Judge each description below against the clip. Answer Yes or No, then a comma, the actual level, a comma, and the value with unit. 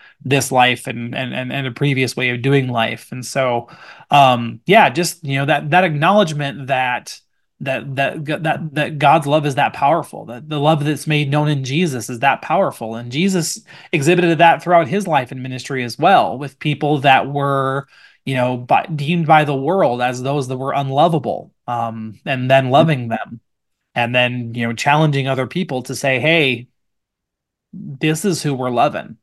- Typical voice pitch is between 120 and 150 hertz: Yes, medium, 140 Hz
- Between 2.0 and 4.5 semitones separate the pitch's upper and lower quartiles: Yes, average, 3.5 semitones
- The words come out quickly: No, average, 185 wpm